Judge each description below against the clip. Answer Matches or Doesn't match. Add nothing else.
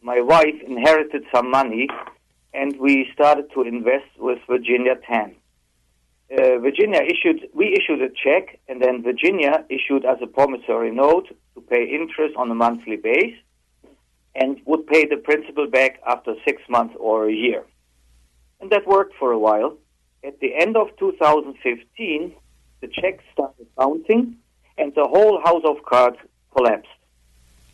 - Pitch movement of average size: Doesn't match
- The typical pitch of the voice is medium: Doesn't match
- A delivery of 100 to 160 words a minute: Matches